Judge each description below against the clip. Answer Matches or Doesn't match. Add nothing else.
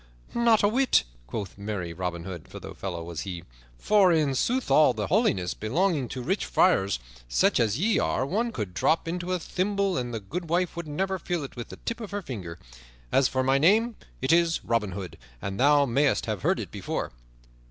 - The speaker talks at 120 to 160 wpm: Doesn't match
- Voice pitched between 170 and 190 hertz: Doesn't match